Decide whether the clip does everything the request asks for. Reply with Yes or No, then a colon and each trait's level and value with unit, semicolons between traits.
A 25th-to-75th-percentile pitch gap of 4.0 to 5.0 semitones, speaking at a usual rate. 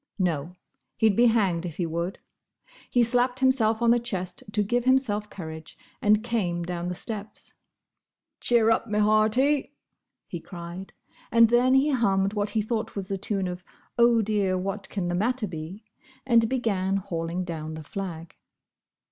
Yes: average, 4.5 semitones; average, 165 wpm